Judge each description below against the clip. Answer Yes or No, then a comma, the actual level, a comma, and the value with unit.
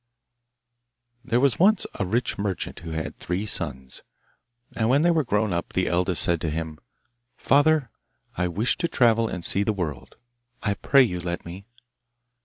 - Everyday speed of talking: Yes, average, 170 wpm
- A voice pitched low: Yes, low, 100 Hz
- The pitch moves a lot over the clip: Yes, wide, 6.2 semitones